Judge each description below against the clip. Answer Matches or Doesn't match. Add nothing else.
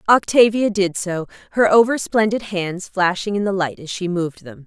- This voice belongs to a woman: Matches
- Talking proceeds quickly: Doesn't match